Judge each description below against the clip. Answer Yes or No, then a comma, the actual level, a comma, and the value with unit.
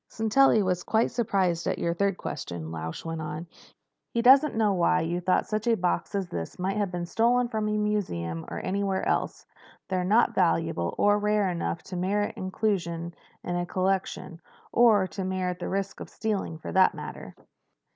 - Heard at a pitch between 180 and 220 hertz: Yes, high, 190 Hz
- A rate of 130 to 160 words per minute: No, average, 175 wpm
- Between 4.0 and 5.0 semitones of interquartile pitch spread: No, average, 3.5 semitones